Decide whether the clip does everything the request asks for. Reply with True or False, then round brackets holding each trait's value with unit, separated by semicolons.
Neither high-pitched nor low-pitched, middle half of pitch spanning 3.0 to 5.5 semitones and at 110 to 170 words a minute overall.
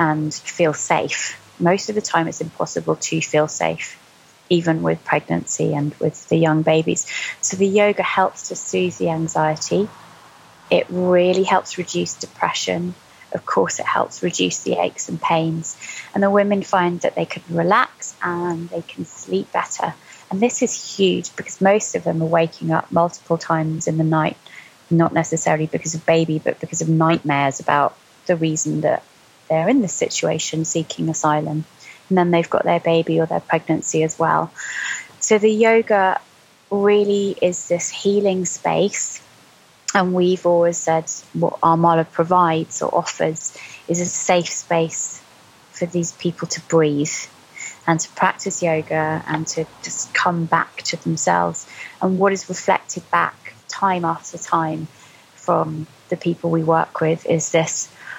False (165 Hz; 2.5 semitones; 160 wpm)